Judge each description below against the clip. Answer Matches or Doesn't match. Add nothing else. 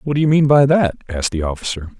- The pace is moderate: Doesn't match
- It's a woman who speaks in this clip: Doesn't match